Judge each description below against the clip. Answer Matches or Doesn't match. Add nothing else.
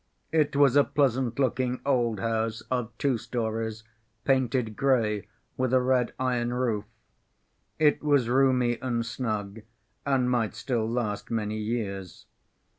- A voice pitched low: Matches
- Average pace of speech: Doesn't match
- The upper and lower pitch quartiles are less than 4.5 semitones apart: Matches